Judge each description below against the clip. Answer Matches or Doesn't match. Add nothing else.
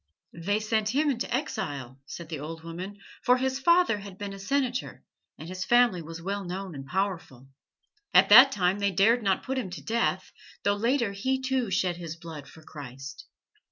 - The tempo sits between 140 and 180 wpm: Doesn't match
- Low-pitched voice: Doesn't match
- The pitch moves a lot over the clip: Matches